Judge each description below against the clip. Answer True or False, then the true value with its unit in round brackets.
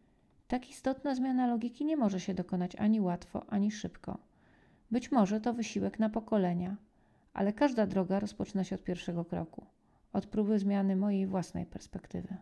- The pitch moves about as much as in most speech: True (3.5 semitones)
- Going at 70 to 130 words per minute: False (155 wpm)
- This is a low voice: False (205 Hz)